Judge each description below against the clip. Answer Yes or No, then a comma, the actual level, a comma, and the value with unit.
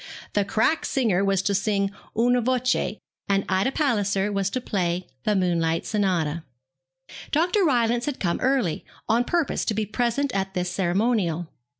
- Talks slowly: No, average, 155 wpm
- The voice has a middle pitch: No, high, 205 Hz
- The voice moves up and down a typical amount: Yes, average, 4.6 semitones